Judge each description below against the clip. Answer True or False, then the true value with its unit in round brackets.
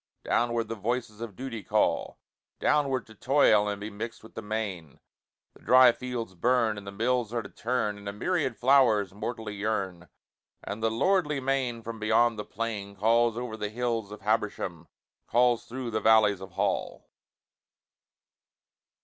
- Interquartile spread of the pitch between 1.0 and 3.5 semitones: True (2.9 semitones)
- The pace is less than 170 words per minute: True (160 wpm)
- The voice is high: False (110 Hz)